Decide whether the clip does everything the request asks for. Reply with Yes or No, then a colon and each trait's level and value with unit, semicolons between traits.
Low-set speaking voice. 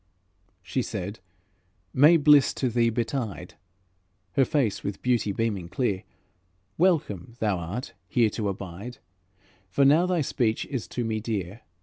Yes: low, 115 Hz